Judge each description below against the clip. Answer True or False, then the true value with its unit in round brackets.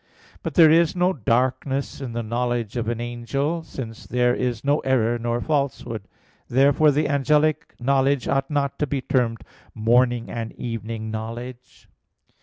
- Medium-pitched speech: False (125 Hz)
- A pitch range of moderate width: True (3.3 semitones)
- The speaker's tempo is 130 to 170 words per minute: True (150 wpm)